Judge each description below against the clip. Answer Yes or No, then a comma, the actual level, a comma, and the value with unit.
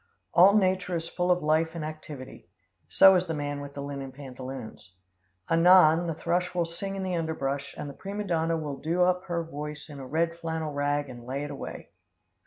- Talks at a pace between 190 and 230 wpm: Yes, average, 200 wpm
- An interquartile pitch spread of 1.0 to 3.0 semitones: No, average, 3.6 semitones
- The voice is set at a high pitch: No, medium, 160 Hz